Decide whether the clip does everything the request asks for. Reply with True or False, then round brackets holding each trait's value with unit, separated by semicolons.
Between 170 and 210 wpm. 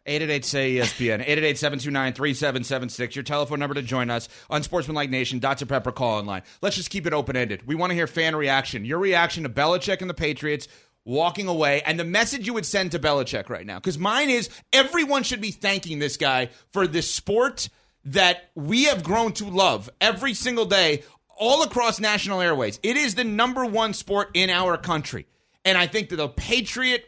True (200 wpm)